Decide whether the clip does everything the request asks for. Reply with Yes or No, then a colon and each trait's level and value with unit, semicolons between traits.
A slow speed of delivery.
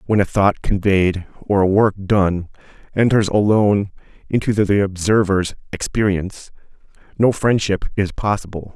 Yes: slow, 125 wpm